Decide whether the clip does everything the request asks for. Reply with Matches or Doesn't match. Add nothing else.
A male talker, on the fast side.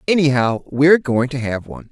Doesn't match